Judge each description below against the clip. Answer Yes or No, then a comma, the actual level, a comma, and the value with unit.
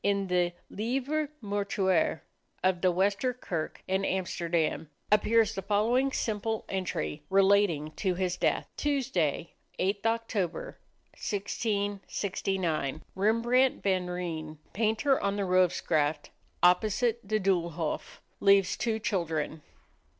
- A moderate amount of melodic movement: Yes, average, 3.5 semitones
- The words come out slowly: Yes, slow, 105 wpm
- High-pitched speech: Yes, high, 195 Hz